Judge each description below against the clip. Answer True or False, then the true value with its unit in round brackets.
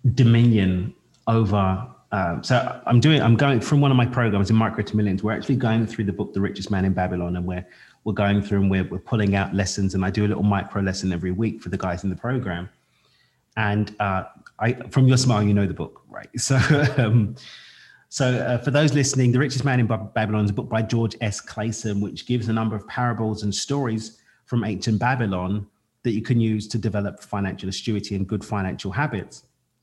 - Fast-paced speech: True (215 wpm)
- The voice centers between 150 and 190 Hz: False (110 Hz)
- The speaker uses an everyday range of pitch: True (3.1 semitones)